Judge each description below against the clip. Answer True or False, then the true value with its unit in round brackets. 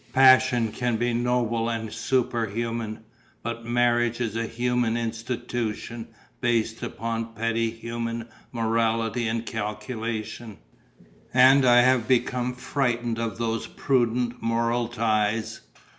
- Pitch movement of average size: False (1.2 semitones)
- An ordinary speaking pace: False (115 wpm)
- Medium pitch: False (115 Hz)